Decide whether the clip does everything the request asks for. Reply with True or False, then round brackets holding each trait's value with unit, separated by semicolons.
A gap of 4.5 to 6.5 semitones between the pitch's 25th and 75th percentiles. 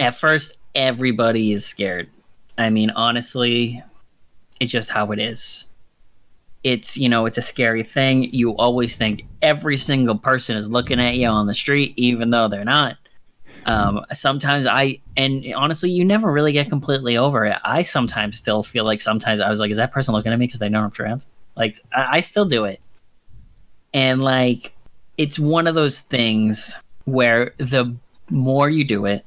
False (3.7 semitones)